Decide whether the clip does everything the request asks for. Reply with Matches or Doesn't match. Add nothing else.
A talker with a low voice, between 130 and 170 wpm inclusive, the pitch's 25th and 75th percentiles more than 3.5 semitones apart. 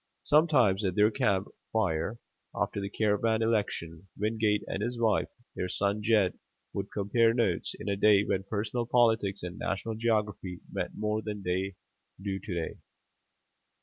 Doesn't match